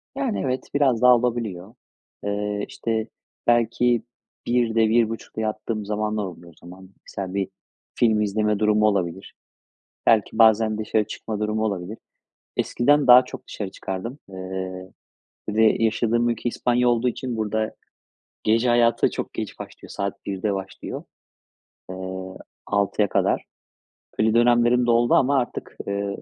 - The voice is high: No, low, 110 Hz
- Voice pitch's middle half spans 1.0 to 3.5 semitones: Yes, average, 3.0 semitones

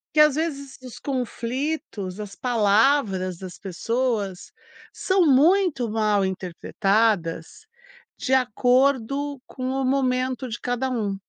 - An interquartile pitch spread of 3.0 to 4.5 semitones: No, average, 5.0 semitones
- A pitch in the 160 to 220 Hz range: No, very high, 250 Hz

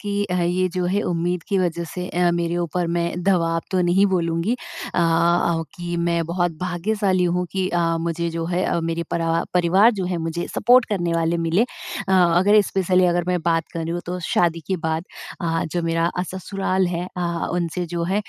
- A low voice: No, medium, 175 Hz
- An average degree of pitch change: No, narrow, 1.6 semitones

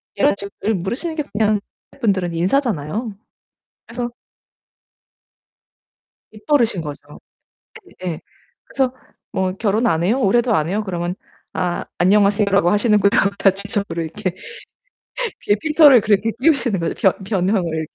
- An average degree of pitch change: Yes, average, 4.5 semitones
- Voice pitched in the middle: No, high, 205 Hz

